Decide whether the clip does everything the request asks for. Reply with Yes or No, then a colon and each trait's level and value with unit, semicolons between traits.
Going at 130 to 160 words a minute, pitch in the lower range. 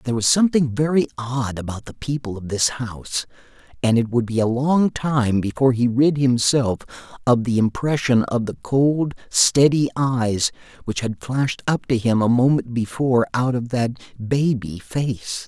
No: average, 170 wpm; low, 125 Hz